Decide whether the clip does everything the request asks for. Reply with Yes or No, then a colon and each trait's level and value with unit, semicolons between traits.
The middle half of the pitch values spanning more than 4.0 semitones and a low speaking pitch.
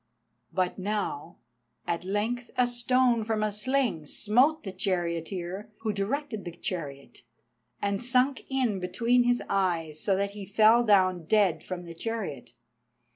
No: average, 4.9 semitones; high, 205 Hz